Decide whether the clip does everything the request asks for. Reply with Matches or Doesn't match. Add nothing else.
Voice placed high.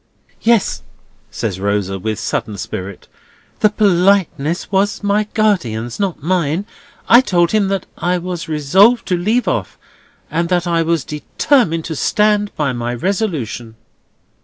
Doesn't match